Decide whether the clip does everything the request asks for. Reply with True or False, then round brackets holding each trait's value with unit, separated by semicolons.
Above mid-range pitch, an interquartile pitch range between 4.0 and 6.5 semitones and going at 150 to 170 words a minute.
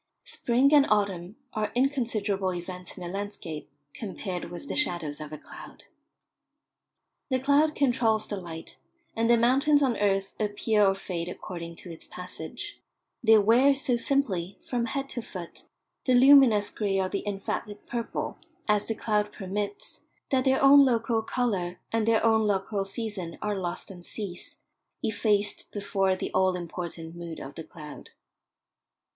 True (205 Hz; 4.5 semitones; 155 wpm)